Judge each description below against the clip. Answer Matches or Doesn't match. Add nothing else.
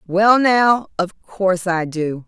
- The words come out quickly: Doesn't match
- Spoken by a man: Doesn't match